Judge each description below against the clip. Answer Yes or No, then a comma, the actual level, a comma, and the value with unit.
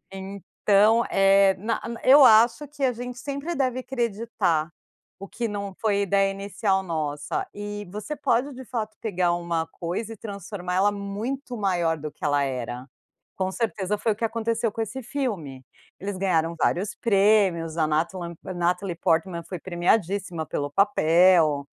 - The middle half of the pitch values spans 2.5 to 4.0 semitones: No, average, 4.7 semitones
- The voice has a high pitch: Yes, high, 195 Hz